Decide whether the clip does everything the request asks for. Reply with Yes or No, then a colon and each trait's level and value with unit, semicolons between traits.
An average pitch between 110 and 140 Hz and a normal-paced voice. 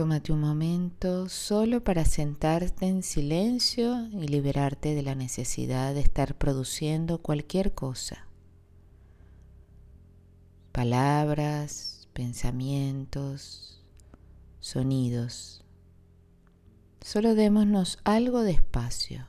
No: low, 135 Hz; slow, 80 wpm